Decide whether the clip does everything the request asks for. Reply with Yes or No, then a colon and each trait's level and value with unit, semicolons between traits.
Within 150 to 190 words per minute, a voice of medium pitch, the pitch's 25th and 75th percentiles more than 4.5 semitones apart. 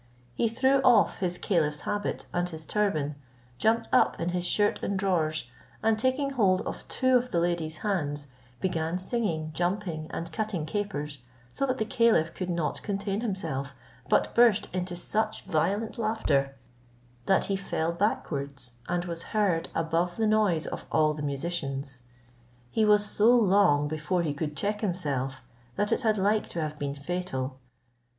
Yes: average, 160 wpm; medium, 180 Hz; average, 5.2 semitones